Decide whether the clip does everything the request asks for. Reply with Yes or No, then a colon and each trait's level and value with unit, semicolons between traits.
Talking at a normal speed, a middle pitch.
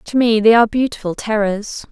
No: average, 190 wpm; high, 220 Hz